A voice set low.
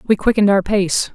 No: high, 200 Hz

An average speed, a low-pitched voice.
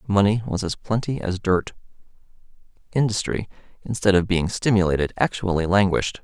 No: slow, 125 wpm; very low, 95 Hz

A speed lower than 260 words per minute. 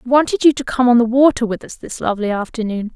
No: fast, 265 wpm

